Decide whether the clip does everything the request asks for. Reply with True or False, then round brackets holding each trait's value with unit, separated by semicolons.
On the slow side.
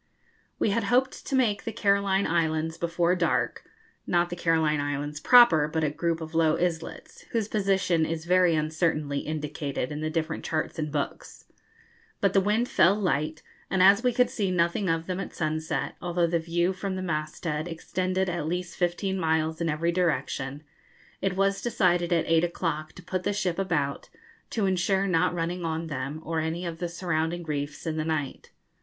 False (185 wpm)